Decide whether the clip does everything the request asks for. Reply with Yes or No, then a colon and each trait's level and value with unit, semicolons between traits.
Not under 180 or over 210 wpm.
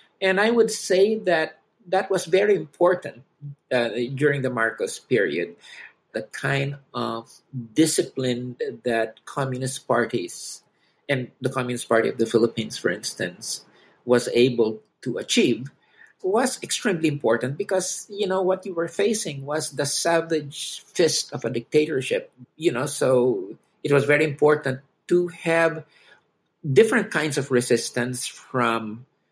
No: slow, 135 wpm